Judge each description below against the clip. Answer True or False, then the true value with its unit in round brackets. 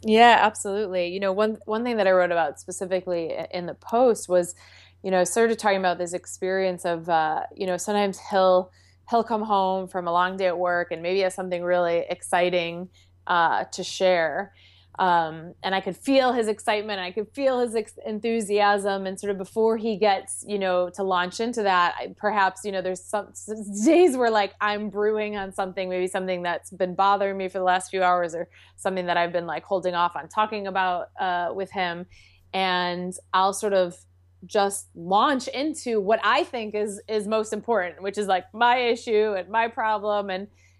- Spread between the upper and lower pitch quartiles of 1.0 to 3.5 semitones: True (3.0 semitones)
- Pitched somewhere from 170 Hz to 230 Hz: True (190 Hz)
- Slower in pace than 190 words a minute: False (200 wpm)